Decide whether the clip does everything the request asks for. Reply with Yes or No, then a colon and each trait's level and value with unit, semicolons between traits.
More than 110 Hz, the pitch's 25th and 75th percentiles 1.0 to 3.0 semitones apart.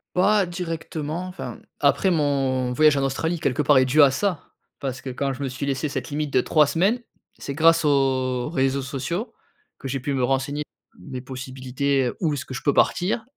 No: medium, 140 Hz; average, 3.4 semitones